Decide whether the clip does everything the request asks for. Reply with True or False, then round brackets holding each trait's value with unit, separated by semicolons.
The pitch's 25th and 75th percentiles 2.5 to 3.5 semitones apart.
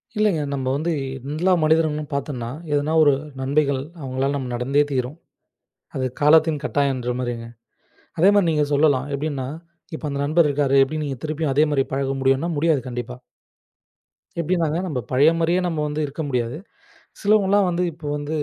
True (3.0 semitones)